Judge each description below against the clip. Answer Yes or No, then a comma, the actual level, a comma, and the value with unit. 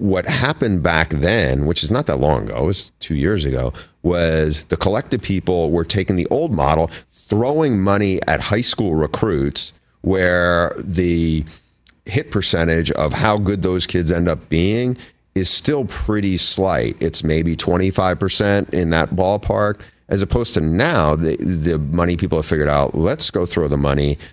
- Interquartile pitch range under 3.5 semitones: No, average, 3.8 semitones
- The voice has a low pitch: Yes, very low, 90 Hz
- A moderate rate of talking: Yes, average, 170 wpm